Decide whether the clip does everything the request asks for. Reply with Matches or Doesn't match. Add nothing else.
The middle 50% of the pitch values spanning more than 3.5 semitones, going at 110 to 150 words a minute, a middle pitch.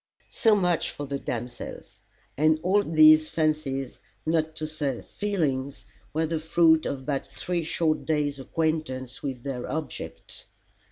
Doesn't match